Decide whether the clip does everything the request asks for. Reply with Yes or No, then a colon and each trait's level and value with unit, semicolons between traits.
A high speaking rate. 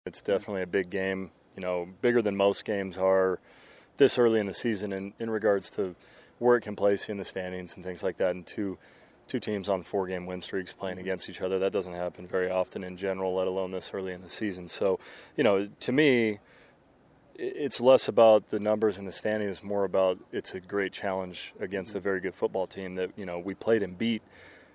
Yes: fast, 220 wpm